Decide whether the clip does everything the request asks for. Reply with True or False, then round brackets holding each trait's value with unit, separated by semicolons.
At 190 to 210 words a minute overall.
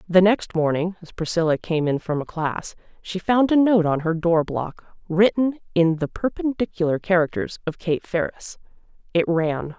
False (170 wpm)